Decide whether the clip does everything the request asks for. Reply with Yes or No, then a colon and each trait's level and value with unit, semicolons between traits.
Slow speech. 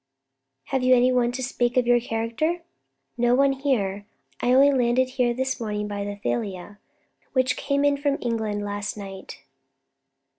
No: average, 155 wpm